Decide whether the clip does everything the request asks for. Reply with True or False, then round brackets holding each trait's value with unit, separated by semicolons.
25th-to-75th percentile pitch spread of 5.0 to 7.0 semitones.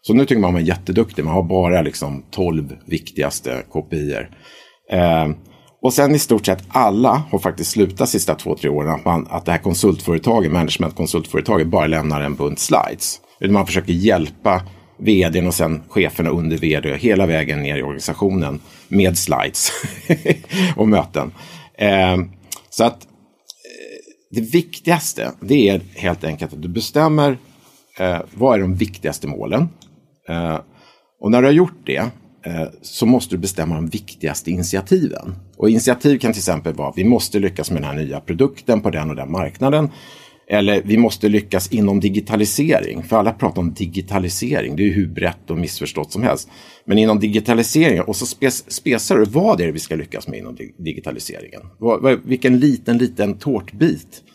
True (5.5 semitones)